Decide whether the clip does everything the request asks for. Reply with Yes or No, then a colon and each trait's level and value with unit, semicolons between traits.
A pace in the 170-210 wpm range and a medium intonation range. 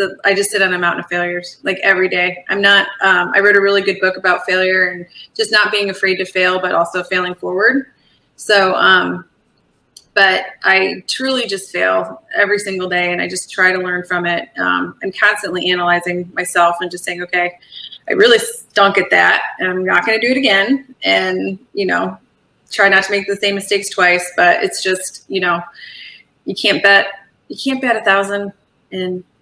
No: average, 200 wpm; narrow, 1.9 semitones